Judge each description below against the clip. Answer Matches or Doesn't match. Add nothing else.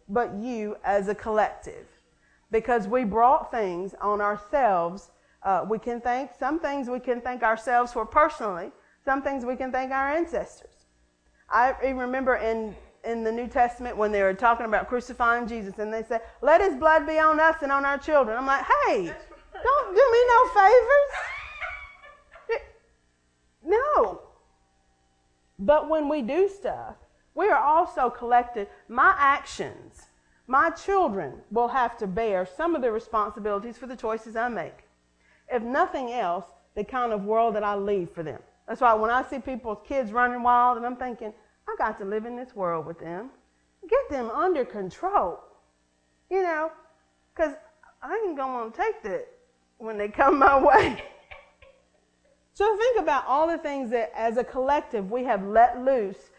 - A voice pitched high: Matches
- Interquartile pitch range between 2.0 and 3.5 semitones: Doesn't match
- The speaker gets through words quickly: Doesn't match